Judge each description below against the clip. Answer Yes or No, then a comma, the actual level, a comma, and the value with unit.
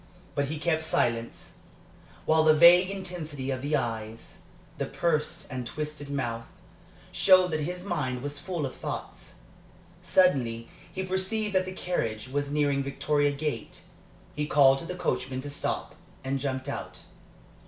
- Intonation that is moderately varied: Yes, average, 4.6 semitones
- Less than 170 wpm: Yes, average, 150 wpm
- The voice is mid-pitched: Yes, medium, 145 Hz